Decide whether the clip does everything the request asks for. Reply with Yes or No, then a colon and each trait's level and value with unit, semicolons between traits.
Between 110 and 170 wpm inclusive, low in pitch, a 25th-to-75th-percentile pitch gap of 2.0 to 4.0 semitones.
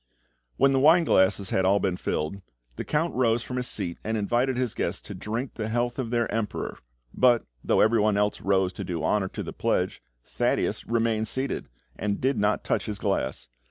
No: average, 195 wpm; low, 110 Hz; average, 3.7 semitones